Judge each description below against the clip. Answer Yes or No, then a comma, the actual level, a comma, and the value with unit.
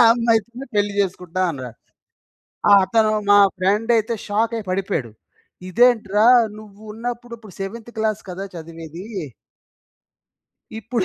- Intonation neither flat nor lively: Yes, average, 3.6 semitones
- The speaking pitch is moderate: No, high, 210 Hz